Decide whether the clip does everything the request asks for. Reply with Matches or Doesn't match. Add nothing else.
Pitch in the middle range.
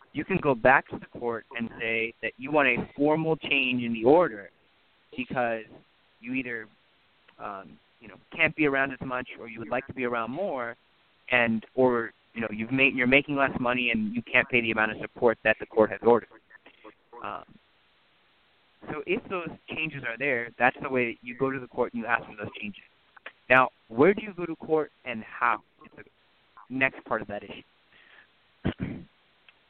Doesn't match